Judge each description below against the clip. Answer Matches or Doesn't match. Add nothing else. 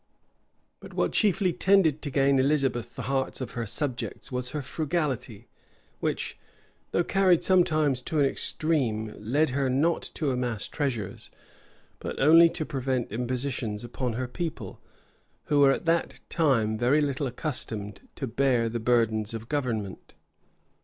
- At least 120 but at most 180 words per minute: Matches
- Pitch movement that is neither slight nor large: Matches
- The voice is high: Doesn't match